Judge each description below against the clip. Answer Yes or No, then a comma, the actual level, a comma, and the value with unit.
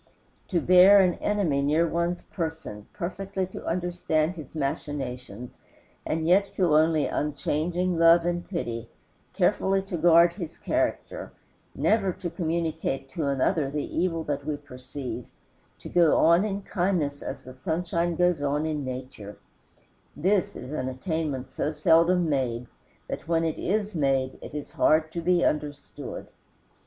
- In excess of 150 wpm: No, average, 140 wpm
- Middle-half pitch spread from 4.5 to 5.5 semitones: No, average, 3.7 semitones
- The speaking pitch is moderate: Yes, medium, 160 Hz